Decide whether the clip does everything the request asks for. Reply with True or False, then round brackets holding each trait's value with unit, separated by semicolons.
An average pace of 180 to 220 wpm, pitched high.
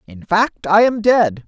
True (205 wpm; 195 Hz)